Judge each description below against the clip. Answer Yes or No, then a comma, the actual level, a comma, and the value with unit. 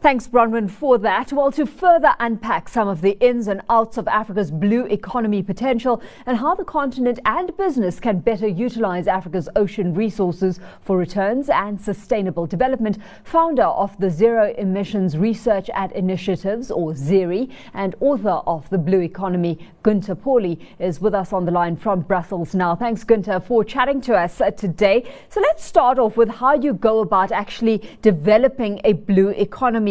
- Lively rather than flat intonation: No, average, 4.3 semitones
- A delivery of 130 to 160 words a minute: No, average, 170 wpm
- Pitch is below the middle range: No, high, 210 Hz